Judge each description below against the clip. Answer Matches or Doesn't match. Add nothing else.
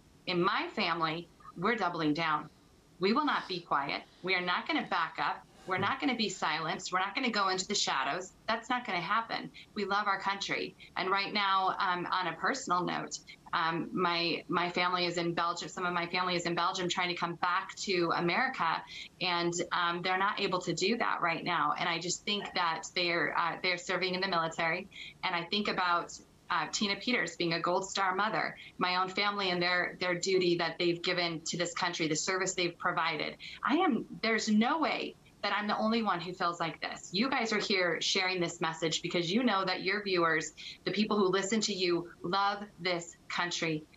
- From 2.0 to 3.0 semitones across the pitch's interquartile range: Matches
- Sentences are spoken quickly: Matches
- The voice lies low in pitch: Doesn't match